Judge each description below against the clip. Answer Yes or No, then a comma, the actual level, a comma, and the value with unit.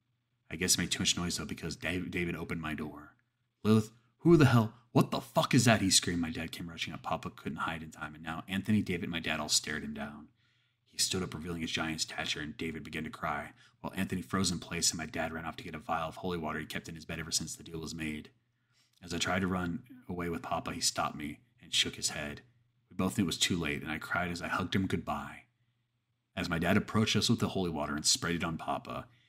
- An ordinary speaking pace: No, fast, 265 wpm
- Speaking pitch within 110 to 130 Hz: No, very low, 95 Hz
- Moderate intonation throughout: No, wide, 6.2 semitones